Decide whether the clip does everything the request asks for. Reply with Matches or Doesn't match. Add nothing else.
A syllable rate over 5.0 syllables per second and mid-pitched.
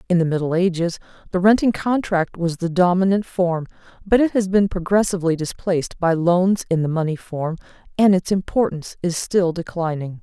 Matches